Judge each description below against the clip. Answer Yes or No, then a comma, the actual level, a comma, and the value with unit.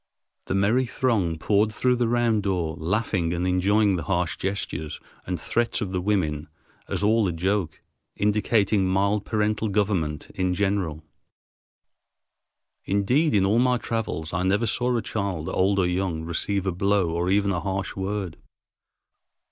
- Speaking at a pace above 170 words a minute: No, average, 155 wpm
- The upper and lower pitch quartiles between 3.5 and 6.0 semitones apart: No, average, 3.0 semitones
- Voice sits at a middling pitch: No, low, 100 Hz